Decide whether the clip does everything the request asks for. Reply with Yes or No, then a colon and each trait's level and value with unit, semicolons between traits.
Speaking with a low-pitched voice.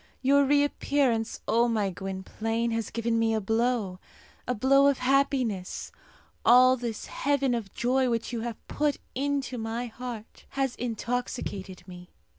No: high, 235 Hz